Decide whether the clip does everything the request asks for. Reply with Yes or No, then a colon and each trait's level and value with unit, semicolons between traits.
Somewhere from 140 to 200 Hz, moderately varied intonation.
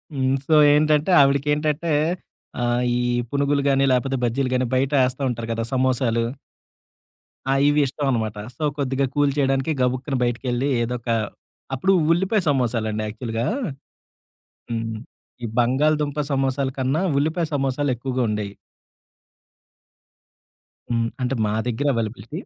No: low, 130 Hz; average, 3.1 semitones